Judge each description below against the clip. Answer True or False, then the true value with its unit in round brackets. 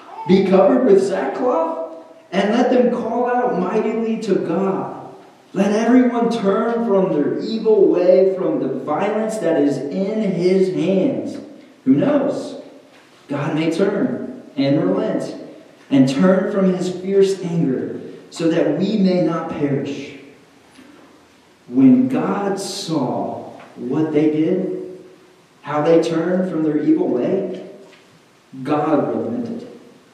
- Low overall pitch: False (190 Hz)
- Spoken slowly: True (120 wpm)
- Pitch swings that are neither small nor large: False (6.2 semitones)